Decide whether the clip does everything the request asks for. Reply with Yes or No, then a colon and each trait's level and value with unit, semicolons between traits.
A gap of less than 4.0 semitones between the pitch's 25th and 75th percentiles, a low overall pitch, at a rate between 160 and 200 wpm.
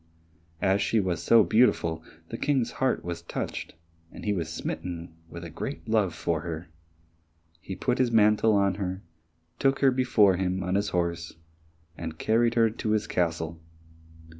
No: average, 4.8 semitones; very low, 95 Hz; average, 165 wpm